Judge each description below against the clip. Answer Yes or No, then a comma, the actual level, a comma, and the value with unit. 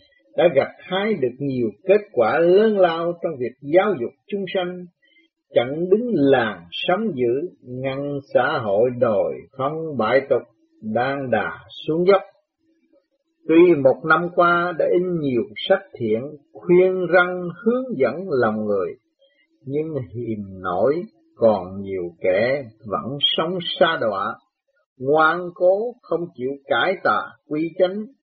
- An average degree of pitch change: No, wide, 6.9 semitones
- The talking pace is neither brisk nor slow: No, slow, 135 wpm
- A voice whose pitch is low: No, medium, 175 Hz